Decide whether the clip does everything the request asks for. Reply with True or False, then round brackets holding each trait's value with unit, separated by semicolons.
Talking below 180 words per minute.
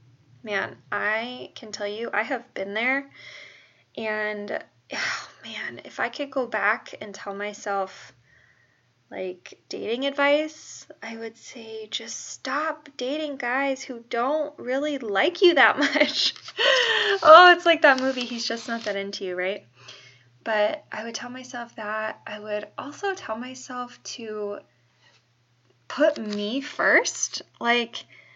True (140 wpm)